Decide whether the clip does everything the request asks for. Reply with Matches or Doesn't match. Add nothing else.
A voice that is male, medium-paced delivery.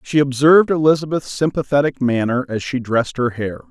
Matches